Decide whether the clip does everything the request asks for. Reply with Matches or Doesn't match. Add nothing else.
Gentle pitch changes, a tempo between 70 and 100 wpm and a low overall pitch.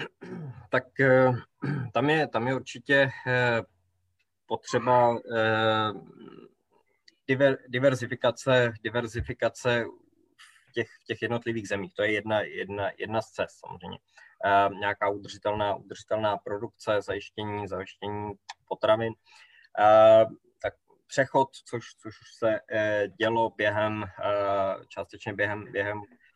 Doesn't match